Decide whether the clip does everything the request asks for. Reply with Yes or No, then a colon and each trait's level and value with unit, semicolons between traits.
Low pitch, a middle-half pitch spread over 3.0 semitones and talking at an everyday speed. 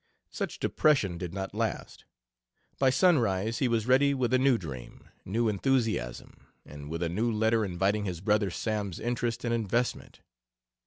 Yes: low, 110 Hz; average, 4.3 semitones; average, 155 wpm